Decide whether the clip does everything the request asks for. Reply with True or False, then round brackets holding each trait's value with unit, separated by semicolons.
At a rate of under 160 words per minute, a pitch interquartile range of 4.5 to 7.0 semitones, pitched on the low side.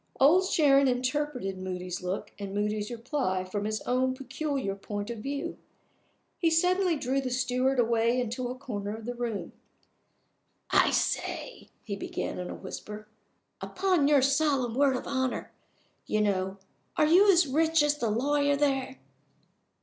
False (150 wpm; 5.2 semitones; 255 Hz)